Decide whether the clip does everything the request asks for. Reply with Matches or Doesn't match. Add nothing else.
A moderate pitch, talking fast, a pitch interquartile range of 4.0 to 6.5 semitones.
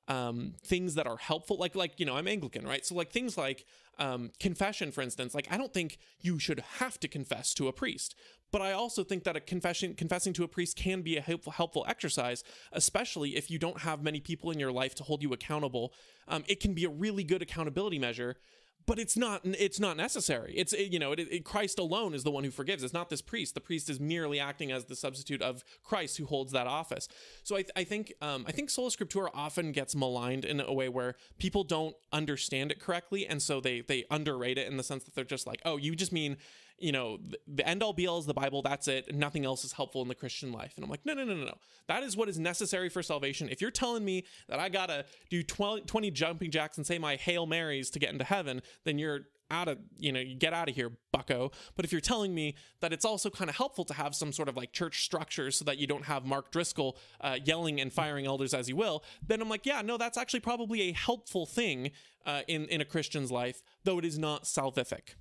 Matches